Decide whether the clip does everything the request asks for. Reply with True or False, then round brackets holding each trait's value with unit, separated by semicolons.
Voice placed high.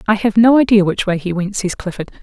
True (200 Hz)